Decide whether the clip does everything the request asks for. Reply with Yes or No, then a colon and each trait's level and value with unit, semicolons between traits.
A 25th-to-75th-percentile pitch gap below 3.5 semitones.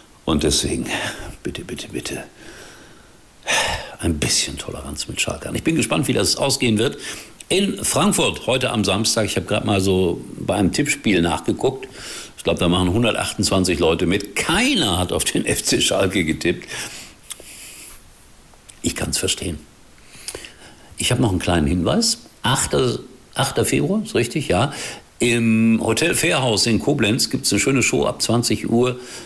No: average, 3.8 semitones